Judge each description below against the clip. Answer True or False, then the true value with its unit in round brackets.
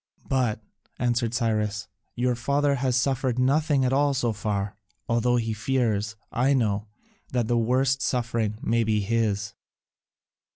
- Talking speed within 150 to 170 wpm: False (135 wpm)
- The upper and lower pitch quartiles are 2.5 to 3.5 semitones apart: True (3.0 semitones)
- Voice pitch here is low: True (120 Hz)